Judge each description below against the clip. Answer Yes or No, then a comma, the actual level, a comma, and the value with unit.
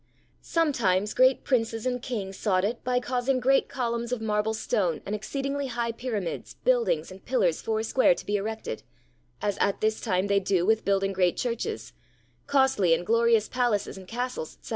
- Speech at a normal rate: Yes, average, 175 wpm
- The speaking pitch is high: Yes, high, 225 Hz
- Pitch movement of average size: Yes, average, 4.0 semitones